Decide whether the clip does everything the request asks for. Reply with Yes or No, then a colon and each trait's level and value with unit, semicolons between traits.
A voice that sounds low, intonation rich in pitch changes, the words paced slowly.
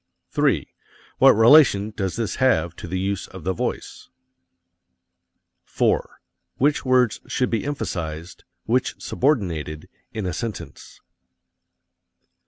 Yes: low, 105 Hz; wide, 6.2 semitones; slow, 110 wpm